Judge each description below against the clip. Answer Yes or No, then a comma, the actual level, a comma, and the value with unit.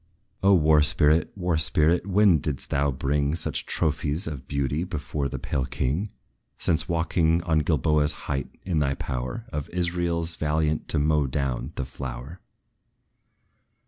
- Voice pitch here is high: No, very low, 75 Hz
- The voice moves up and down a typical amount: Yes, average, 3.1 semitones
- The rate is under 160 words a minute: Yes, average, 145 wpm